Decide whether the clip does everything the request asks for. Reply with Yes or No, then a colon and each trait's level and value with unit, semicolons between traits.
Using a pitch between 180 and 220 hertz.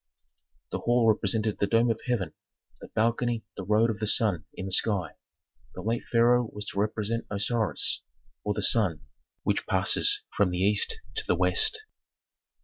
No: low, 110 Hz